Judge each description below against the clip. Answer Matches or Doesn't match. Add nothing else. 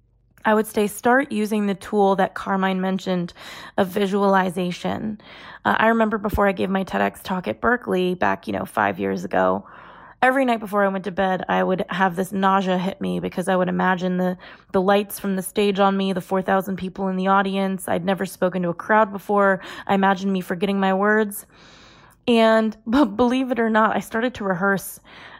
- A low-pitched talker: Doesn't match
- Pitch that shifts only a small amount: Matches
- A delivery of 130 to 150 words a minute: Doesn't match